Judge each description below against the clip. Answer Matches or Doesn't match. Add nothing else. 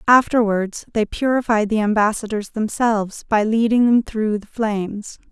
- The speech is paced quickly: Doesn't match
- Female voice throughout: Matches